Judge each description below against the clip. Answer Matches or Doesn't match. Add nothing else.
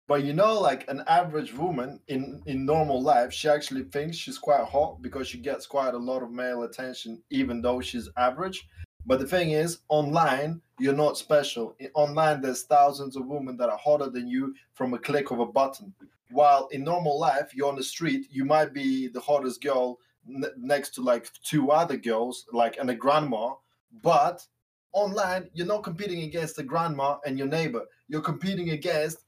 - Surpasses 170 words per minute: Matches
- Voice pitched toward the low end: Doesn't match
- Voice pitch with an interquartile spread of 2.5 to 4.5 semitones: Matches